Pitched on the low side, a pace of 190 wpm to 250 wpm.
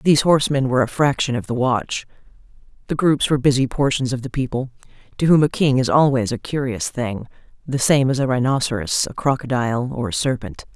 Yes: low, 130 Hz; average, 195 wpm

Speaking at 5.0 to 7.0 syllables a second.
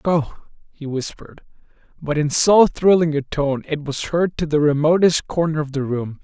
No: 4.8 syllables/s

